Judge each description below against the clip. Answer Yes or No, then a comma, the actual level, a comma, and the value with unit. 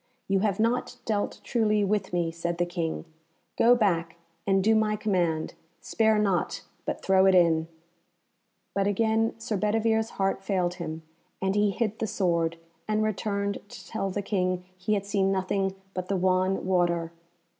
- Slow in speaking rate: No, average, 165 wpm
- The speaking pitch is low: No, high, 195 Hz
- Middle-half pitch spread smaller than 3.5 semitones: Yes, average, 2.9 semitones